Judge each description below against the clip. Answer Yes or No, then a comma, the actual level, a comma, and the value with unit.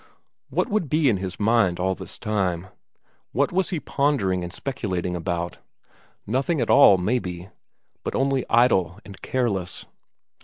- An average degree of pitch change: No, wide, 6.5 semitones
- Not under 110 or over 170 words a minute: Yes, average, 145 wpm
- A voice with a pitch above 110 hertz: No, low, 100 Hz